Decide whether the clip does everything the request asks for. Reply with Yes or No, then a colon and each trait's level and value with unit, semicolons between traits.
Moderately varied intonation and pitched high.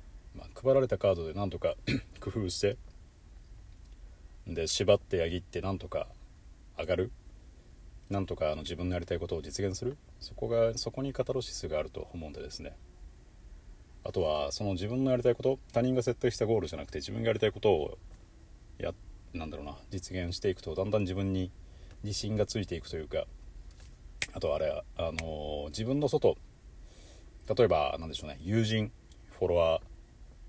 No: average, 5.0 semitones; very low, 90 Hz